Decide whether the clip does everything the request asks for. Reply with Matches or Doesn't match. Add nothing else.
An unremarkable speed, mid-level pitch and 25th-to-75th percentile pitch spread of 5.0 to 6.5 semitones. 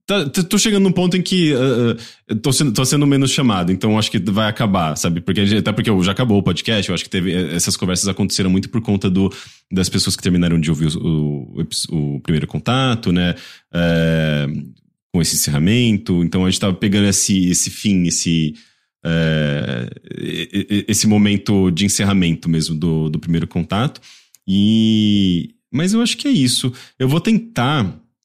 Doesn't match